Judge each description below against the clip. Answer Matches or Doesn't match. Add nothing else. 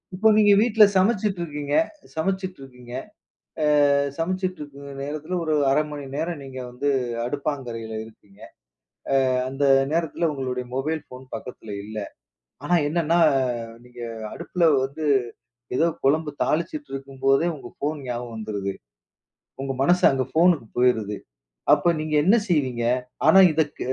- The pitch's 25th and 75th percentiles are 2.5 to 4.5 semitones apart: Doesn't match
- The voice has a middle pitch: Matches